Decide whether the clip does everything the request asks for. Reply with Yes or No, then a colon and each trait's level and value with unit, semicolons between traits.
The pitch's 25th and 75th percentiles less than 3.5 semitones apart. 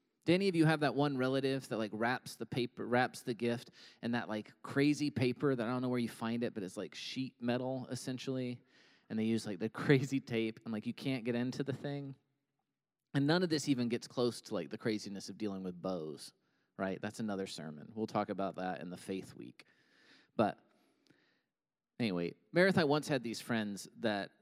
No: average, 4.1 semitones